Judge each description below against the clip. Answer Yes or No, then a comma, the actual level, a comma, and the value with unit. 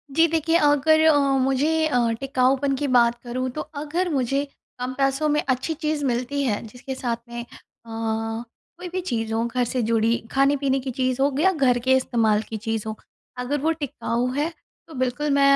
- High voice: Yes, very high, 265 Hz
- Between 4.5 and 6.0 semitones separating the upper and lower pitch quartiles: No, average, 3.5 semitones